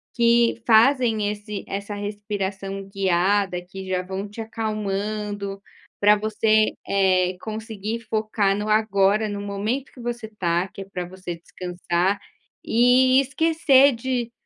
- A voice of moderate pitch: No, high, 205 Hz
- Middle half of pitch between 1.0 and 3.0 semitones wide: Yes, narrow, 2.5 semitones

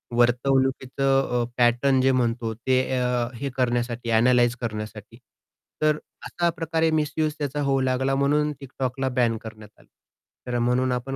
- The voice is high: No, low, 130 Hz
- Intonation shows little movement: Yes, narrow, 2.3 semitones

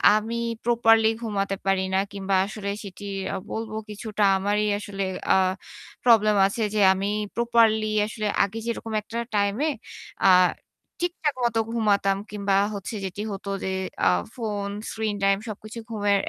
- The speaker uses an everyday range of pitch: No, narrow, 2.1 semitones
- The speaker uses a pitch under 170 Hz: No, high, 210 Hz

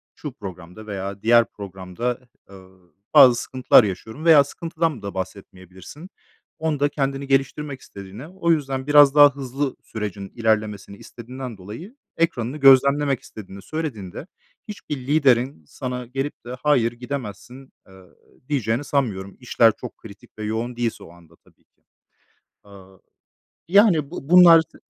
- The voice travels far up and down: Yes, wide, 6.1 semitones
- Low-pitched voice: Yes, low, 125 Hz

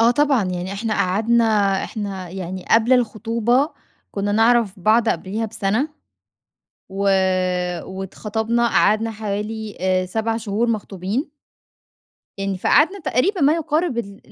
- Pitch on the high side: Yes, high, 220 Hz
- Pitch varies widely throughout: No, average, 3.2 semitones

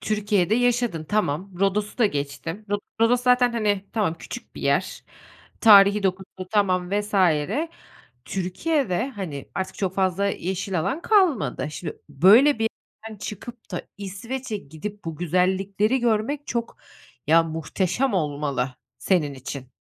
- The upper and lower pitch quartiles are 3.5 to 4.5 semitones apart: Yes, average, 4.2 semitones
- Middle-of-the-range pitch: No, high, 195 Hz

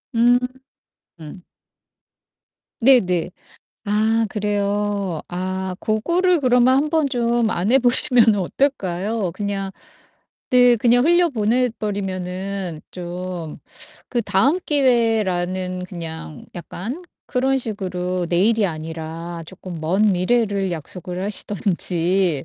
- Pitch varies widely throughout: No, average, 4.9 semitones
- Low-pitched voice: No, high, 200 Hz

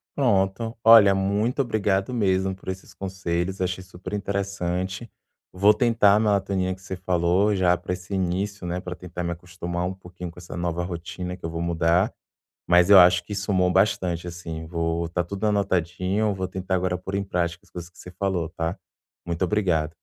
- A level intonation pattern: Yes, narrow, 2.0 semitones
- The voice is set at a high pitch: No, very low, 95 Hz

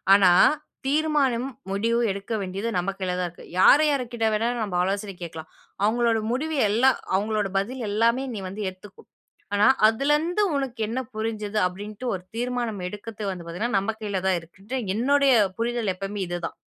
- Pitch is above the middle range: Yes, high, 215 Hz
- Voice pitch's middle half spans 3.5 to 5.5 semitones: Yes, average, 3.9 semitones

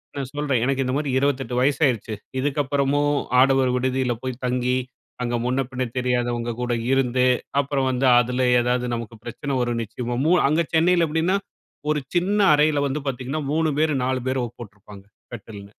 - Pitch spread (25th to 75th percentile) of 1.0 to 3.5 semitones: Yes, average, 2.8 semitones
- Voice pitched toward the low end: Yes, low, 130 Hz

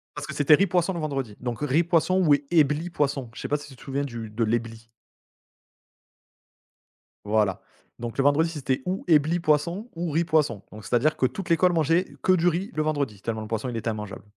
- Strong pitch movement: Yes, wide, 6.1 semitones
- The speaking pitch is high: No, medium, 145 Hz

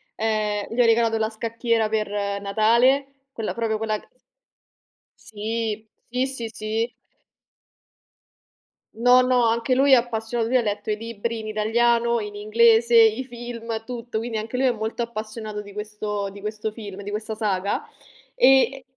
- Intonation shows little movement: Yes, narrow, 1.8 semitones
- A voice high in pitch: Yes, high, 225 Hz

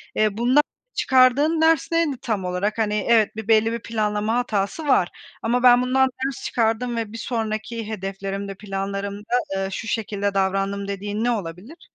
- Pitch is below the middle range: No, high, 215 Hz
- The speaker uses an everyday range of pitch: Yes, average, 3.4 semitones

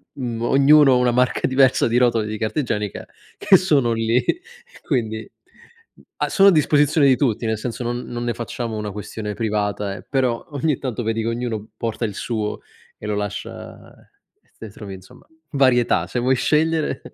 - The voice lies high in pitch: No, low, 120 Hz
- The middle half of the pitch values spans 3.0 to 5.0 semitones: Yes, average, 3.5 semitones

